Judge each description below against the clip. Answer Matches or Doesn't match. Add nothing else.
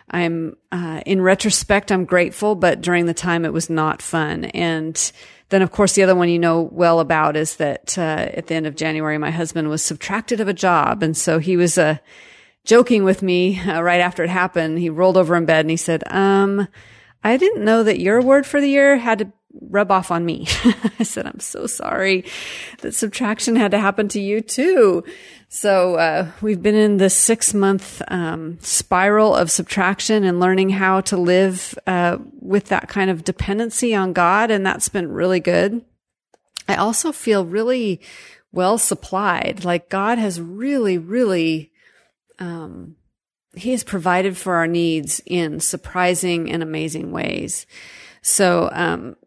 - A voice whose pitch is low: Doesn't match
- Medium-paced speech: Matches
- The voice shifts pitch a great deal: Doesn't match